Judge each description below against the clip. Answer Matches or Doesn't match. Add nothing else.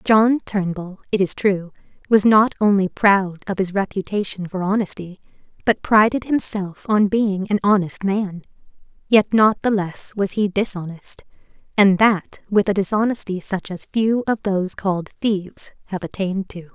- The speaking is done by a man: Doesn't match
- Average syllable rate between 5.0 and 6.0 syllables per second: Doesn't match